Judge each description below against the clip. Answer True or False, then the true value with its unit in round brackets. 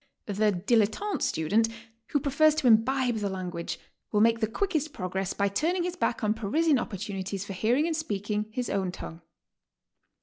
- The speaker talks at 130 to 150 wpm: False (170 wpm)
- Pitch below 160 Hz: False (220 Hz)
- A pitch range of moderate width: False (6.0 semitones)